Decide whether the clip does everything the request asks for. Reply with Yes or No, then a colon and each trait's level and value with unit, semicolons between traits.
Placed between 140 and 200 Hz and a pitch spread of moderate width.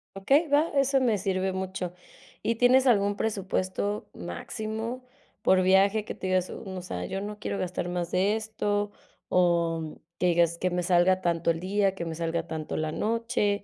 Yes: high, 190 Hz; average, 3.5 semitones